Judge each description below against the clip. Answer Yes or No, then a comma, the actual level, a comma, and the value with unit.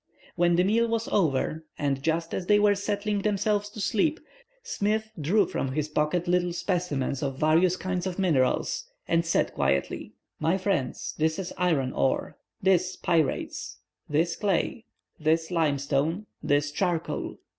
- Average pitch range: Yes, average, 4.6 semitones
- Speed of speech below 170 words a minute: Yes, average, 145 wpm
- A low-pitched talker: No, medium, 175 Hz